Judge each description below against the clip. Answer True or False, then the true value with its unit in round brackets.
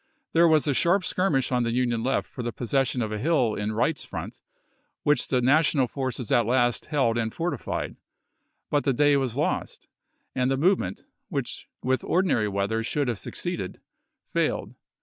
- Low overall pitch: True (130 Hz)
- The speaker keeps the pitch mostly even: False (3.9 semitones)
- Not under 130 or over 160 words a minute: False (170 wpm)